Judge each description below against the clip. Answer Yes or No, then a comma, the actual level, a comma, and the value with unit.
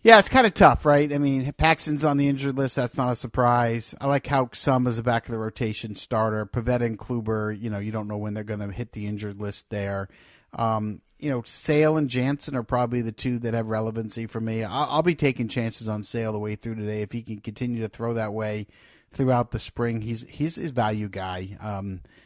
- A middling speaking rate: No, fast, 235 wpm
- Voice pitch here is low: Yes, low, 115 Hz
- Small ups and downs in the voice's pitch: No, average, 3.7 semitones